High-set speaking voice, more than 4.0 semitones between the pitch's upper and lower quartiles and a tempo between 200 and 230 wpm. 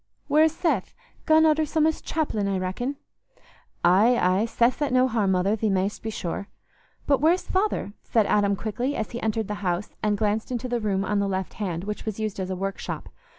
Yes: high, 215 Hz; average, 4.5 semitones; fast, 205 wpm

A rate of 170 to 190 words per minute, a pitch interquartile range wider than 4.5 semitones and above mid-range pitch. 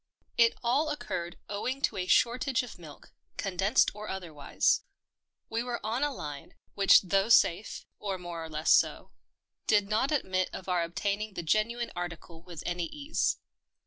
Yes: average, 175 wpm; average, 5.1 semitones; high, 200 Hz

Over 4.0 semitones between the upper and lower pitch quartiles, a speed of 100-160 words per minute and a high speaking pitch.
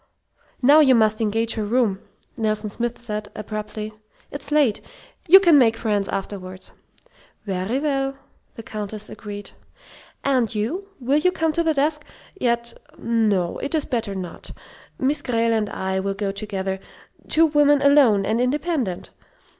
Yes: average, 5.3 semitones; average, 145 wpm; high, 230 Hz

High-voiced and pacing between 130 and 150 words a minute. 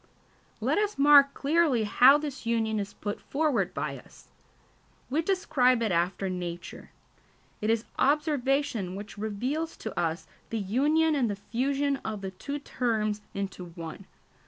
Yes: high, 235 Hz; average, 145 wpm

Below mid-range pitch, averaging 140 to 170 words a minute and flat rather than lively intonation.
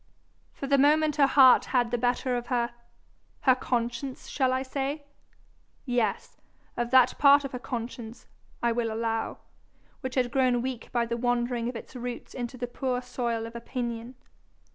No: high, 245 Hz; average, 165 wpm; narrow, 1.8 semitones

